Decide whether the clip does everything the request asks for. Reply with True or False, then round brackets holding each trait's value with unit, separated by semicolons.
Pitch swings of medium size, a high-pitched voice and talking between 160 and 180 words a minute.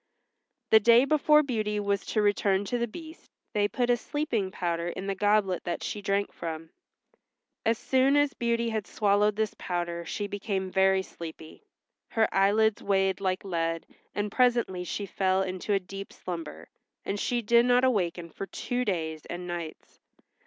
True (4.0 semitones; 200 Hz; 165 wpm)